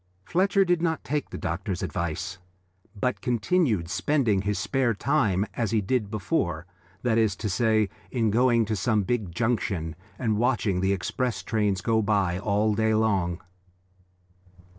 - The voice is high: No, low, 110 Hz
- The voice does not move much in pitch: No, average, 4.1 semitones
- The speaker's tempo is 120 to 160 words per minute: Yes, average, 150 wpm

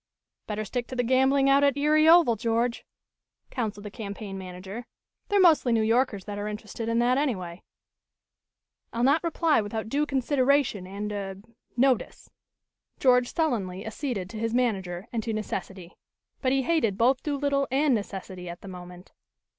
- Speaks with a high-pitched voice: Yes, high, 230 Hz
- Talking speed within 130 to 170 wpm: Yes, average, 160 wpm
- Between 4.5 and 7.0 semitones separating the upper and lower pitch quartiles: Yes, average, 5.1 semitones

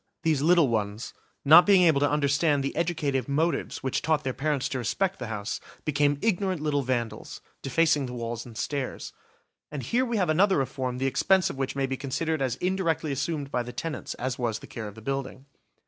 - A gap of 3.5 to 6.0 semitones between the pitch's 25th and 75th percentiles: Yes, average, 4.0 semitones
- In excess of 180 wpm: Yes, fast, 205 wpm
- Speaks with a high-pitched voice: No, medium, 140 Hz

